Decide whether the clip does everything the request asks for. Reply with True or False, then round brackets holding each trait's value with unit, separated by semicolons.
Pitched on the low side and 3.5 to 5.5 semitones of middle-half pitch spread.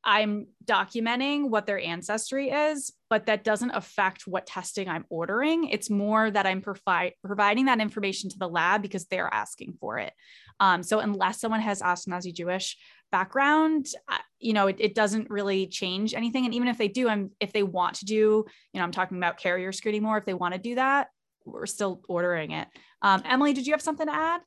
False (210 Hz; 3.8 semitones)